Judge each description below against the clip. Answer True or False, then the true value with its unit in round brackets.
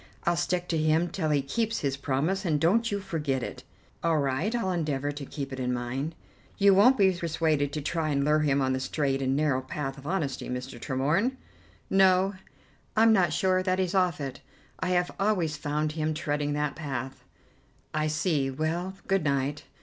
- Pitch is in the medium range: True (155 Hz)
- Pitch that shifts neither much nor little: True (4.7 semitones)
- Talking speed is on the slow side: False (195 wpm)